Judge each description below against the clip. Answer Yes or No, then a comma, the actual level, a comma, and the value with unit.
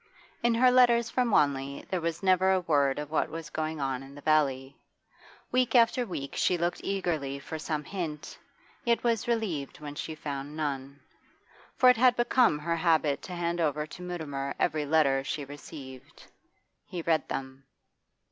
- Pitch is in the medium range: Yes, medium, 155 Hz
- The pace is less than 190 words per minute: Yes, average, 170 wpm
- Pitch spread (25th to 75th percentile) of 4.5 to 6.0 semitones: Yes, average, 4.9 semitones